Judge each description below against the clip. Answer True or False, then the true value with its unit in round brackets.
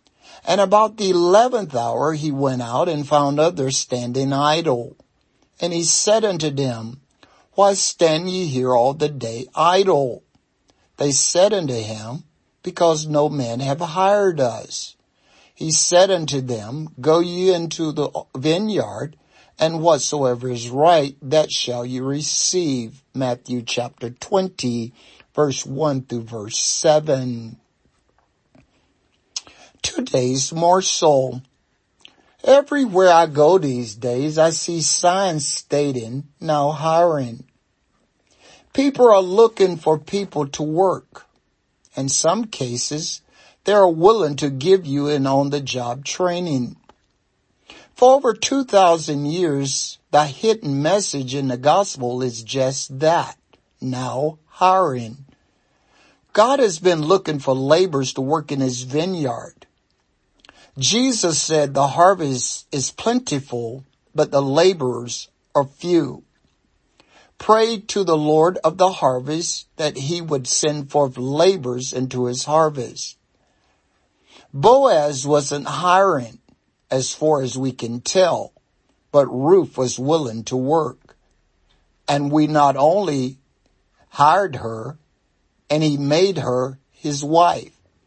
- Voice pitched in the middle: True (145 Hz)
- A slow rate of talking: True (120 wpm)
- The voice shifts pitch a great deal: False (4.6 semitones)